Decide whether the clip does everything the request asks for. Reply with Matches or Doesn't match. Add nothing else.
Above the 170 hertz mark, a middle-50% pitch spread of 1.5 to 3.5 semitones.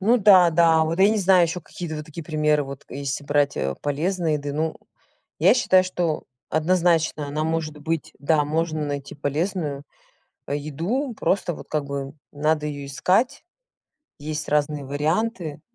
Doesn't match